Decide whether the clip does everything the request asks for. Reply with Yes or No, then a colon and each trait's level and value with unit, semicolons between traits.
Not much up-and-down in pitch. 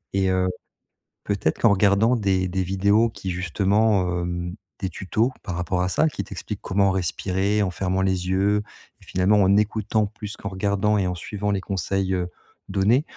Yes: narrow, 1.9 semitones